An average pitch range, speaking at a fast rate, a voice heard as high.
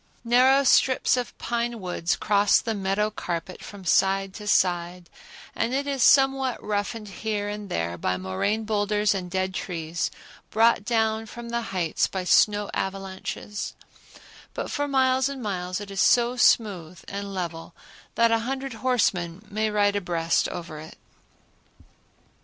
No: average, 4.2 semitones; average, 145 wpm; high, 205 Hz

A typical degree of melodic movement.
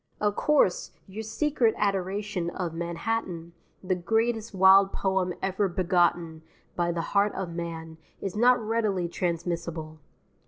Yes: average, 3.6 semitones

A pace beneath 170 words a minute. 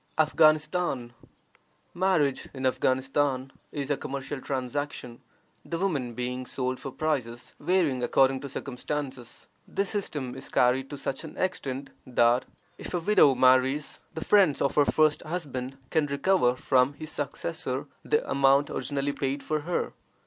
Yes: average, 140 wpm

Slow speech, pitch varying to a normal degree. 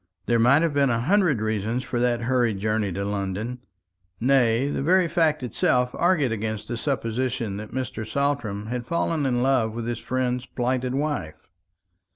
No: average, 170 wpm; average, 3.6 semitones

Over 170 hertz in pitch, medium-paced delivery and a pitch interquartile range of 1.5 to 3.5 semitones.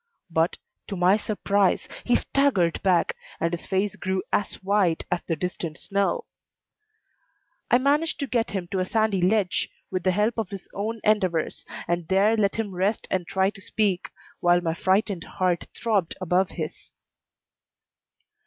Yes: high, 190 Hz; average, 160 wpm; average, 3.0 semitones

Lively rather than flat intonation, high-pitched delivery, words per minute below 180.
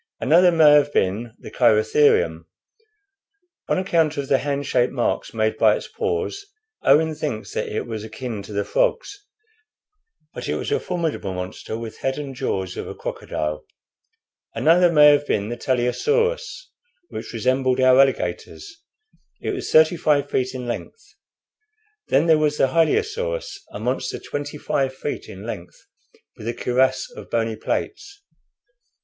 No: wide, 6.1 semitones; low, 135 Hz; average, 155 wpm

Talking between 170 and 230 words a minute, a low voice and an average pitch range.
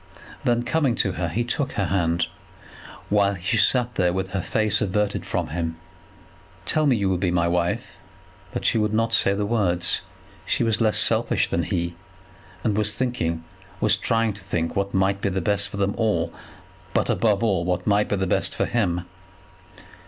Yes: average, 180 wpm; low, 100 Hz; average, 3.7 semitones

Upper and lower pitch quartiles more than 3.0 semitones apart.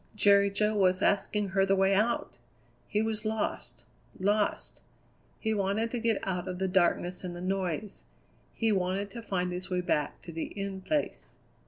No: narrow, 2.4 semitones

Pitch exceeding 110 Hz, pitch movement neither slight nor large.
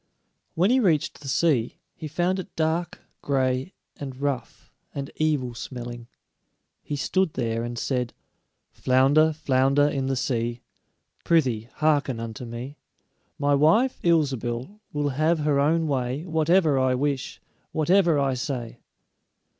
Yes: medium, 140 Hz; average, 3.8 semitones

